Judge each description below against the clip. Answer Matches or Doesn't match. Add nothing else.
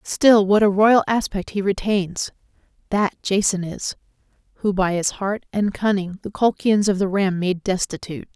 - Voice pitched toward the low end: Doesn't match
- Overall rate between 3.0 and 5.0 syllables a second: Matches